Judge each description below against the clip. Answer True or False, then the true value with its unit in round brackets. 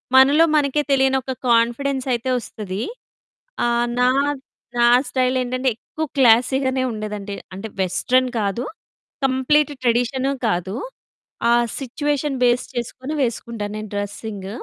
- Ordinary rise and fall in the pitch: True (3.2 semitones)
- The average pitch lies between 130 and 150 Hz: False (245 Hz)